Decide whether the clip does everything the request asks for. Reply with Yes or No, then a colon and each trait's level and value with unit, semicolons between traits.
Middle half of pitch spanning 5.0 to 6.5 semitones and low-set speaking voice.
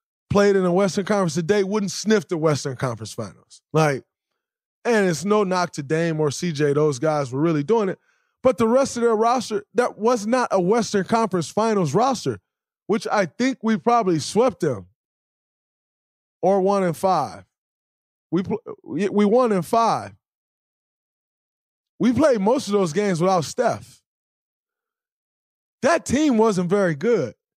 No: average, 5.3 semitones; high, 205 Hz